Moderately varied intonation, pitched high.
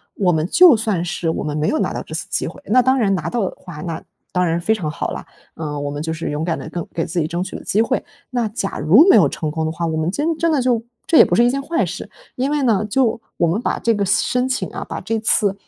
No: wide, 7.1 semitones; high, 195 Hz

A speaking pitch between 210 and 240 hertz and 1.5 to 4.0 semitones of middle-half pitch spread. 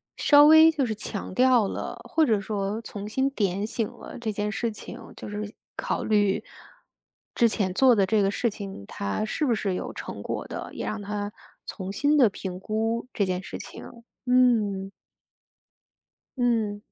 Yes: high, 215 Hz; average, 3.2 semitones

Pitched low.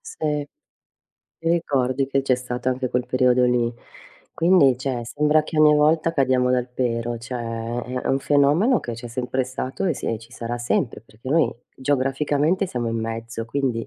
Yes: low, 130 Hz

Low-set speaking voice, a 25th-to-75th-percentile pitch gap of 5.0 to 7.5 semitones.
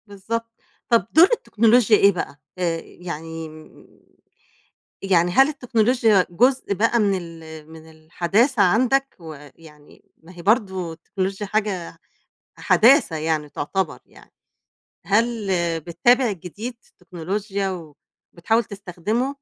No: high, 195 Hz; wide, 5.5 semitones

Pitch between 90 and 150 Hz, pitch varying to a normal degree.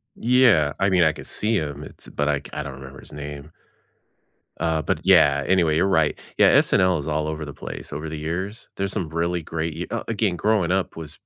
No: very low, 80 Hz; average, 4.0 semitones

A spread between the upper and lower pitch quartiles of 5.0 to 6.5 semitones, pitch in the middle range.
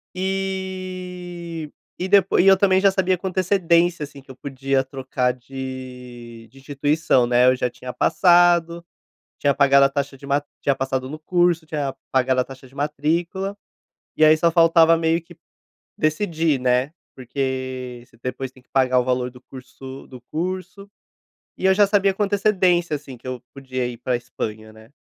Yes: wide, 5.4 semitones; medium, 145 Hz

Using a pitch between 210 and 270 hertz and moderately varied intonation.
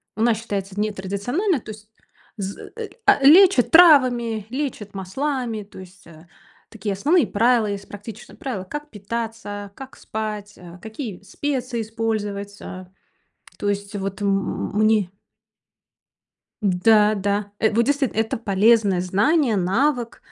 Yes: high, 215 Hz; average, 3.4 semitones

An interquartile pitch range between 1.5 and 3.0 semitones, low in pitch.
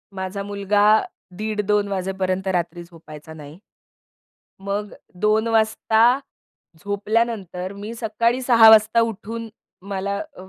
No: average, 2.7 semitones; high, 205 Hz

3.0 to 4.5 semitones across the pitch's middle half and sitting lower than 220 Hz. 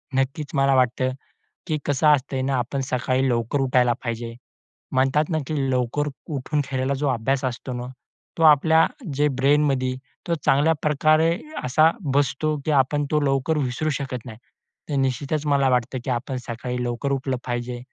No: narrow, 2.6 semitones; low, 135 Hz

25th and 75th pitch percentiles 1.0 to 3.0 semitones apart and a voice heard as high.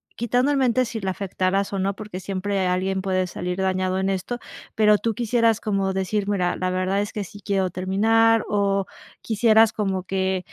Yes: narrow, 2.6 semitones; high, 195 Hz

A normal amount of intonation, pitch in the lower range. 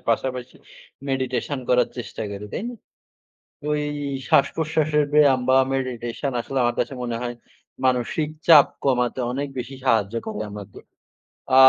Yes: average, 3.0 semitones; low, 130 Hz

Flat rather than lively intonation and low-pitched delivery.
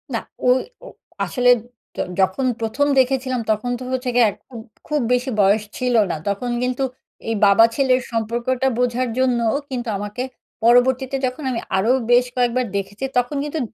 No: narrow, 2.3 semitones; high, 245 Hz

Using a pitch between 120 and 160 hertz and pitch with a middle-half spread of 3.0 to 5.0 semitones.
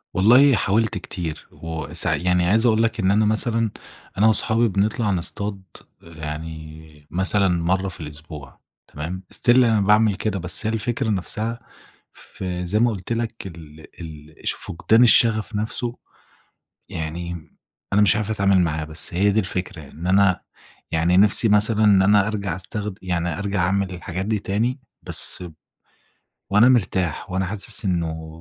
No: very low, 95 Hz; average, 4.1 semitones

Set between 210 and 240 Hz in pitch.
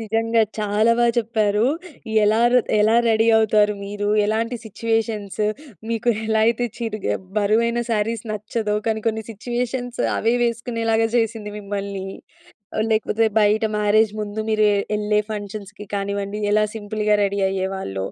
Yes: high, 215 Hz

